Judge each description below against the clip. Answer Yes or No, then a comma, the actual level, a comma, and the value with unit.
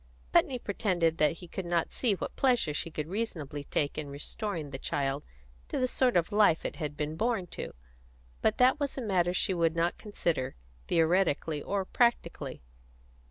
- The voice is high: No, medium, 170 Hz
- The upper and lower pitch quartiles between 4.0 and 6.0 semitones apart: Yes, wide, 5.4 semitones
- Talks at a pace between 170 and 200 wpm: Yes, average, 175 wpm